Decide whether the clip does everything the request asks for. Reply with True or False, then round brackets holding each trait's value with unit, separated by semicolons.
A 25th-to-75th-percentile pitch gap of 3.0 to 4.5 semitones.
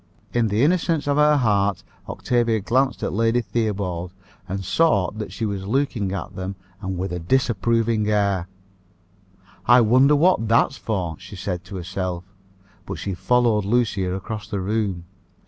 True (4.0 semitones)